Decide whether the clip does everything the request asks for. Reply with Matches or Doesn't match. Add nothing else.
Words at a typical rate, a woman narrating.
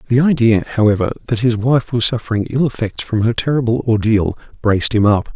Doesn't match